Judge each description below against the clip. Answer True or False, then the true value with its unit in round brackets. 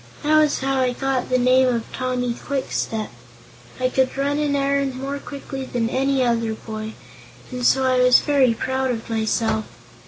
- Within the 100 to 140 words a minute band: False (175 wpm)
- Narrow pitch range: True (2.1 semitones)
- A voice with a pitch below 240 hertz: False (255 Hz)